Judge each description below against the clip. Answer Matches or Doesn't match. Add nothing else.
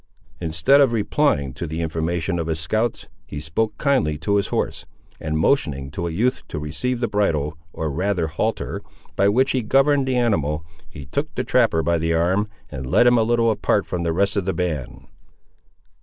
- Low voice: Matches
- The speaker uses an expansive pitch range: Matches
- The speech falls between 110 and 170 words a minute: Doesn't match